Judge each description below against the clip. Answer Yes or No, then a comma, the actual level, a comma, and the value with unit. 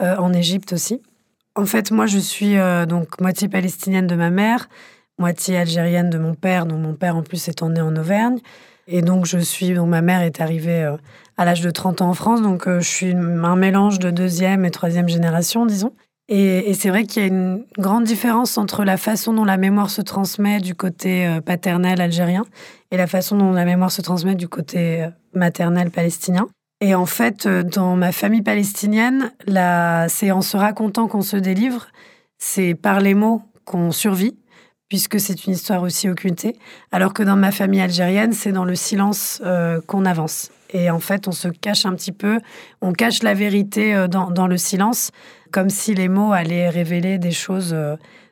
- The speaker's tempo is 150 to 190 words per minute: No, average, 200 wpm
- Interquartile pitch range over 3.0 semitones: No, average, 2.7 semitones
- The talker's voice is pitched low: No, medium, 185 Hz